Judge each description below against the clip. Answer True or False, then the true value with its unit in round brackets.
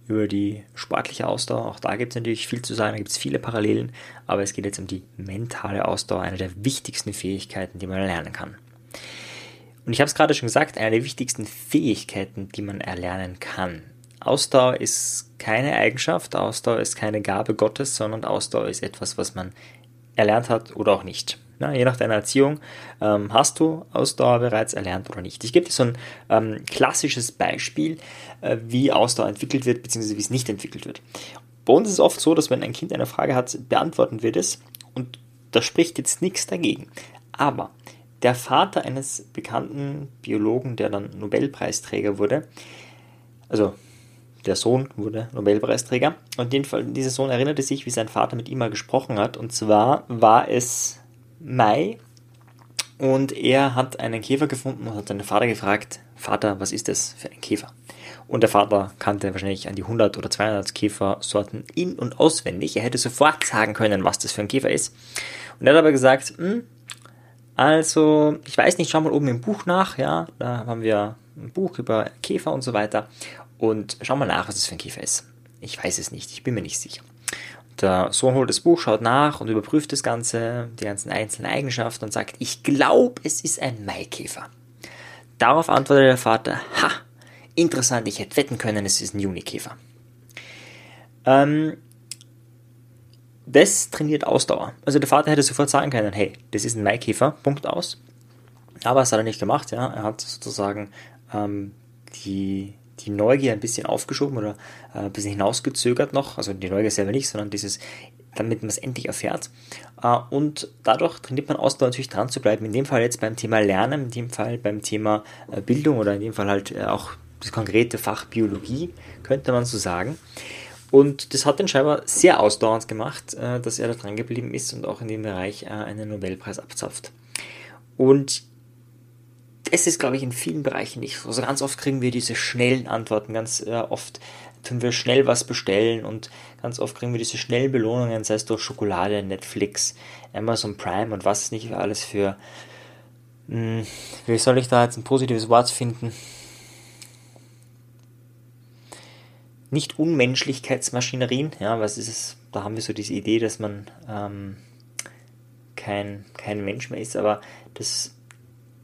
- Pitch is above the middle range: False (120 Hz)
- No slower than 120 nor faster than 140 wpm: False (175 wpm)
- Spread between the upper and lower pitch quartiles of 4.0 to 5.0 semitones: False (3.3 semitones)